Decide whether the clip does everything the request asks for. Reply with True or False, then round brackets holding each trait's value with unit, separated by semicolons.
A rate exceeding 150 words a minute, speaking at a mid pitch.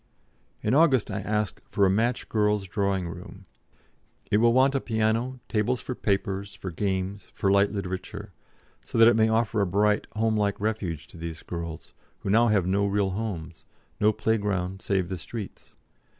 False (170 wpm; 100 Hz)